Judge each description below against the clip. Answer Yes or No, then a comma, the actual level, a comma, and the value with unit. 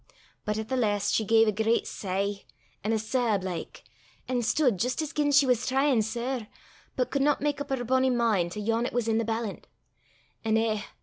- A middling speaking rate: No, fast, 210 wpm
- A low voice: No, high, 230 Hz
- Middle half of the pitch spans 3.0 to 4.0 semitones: Yes, average, 3.3 semitones